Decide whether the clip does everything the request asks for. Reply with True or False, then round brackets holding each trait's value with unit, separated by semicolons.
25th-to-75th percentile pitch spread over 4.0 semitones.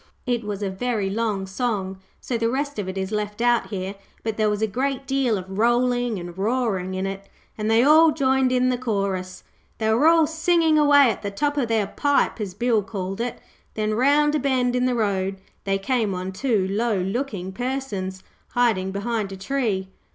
True (4.6 semitones)